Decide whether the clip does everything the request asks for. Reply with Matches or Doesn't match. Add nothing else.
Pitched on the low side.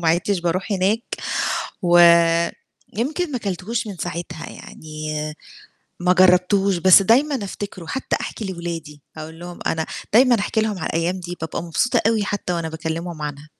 Doesn't match